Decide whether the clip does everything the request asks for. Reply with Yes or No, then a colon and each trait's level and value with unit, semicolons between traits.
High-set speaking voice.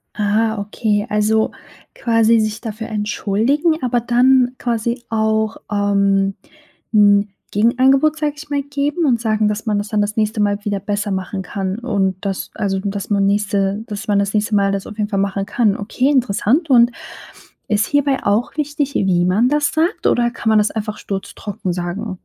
Yes: high, 215 Hz